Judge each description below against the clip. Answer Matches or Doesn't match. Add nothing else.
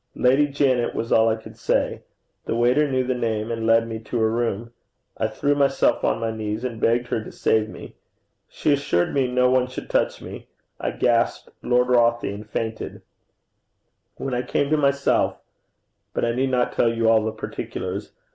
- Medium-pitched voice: Doesn't match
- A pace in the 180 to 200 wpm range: Matches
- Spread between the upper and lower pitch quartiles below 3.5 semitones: Matches